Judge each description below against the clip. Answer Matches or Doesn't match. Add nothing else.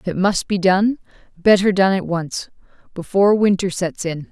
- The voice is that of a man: Doesn't match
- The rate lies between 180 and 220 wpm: Doesn't match